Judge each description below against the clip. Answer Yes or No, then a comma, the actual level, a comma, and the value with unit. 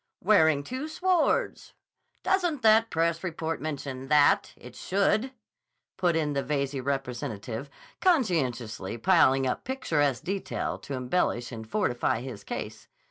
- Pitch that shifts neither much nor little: No, wide, 7.6 semitones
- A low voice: No, medium, 150 Hz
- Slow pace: Yes, slow, 125 wpm